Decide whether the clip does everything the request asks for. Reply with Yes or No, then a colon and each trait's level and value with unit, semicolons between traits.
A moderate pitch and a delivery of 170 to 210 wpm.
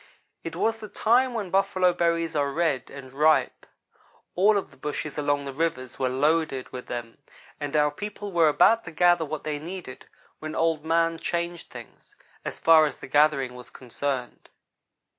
Yes: medium, 155 Hz; average, 175 wpm